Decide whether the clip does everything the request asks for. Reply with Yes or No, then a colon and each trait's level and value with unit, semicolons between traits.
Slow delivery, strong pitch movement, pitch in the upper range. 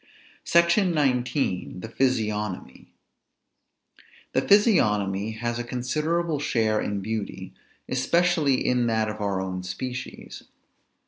No: slow, 105 wpm; wide, 5.8 semitones; low, 120 Hz